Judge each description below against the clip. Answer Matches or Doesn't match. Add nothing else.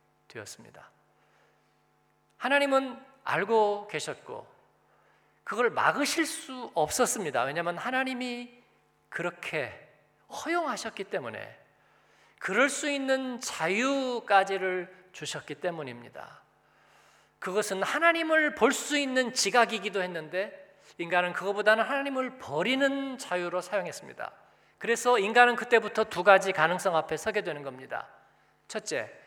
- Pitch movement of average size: Doesn't match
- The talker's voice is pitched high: Matches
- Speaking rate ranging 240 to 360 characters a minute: Matches